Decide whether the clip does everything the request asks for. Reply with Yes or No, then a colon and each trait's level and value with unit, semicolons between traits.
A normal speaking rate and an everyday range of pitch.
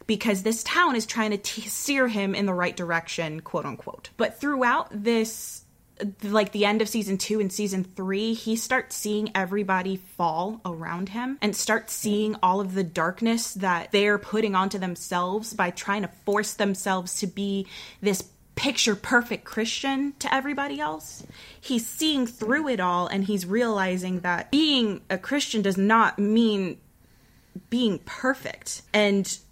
Yes: average, 155 wpm; average, 3.1 semitones